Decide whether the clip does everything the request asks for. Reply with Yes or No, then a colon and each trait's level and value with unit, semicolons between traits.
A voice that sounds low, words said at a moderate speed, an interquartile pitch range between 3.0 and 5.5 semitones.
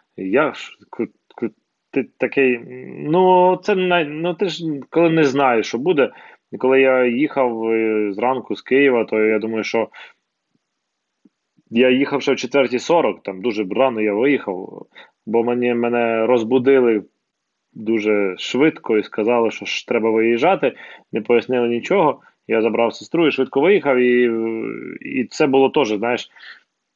Yes: low, 125 Hz; average, 130 wpm; average, 3.7 semitones